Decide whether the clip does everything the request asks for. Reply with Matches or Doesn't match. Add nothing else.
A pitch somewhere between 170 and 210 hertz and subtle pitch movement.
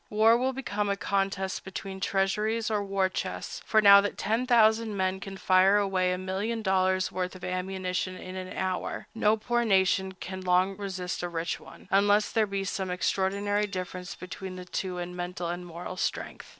Matches